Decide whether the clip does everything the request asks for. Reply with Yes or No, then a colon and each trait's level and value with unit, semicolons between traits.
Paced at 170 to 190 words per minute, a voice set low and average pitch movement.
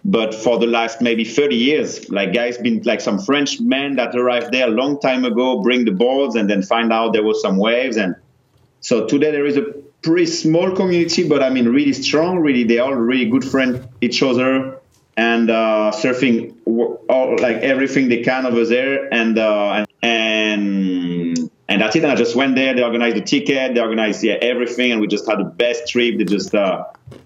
No: fast, 205 wpm; low, 120 Hz; average, 3.1 semitones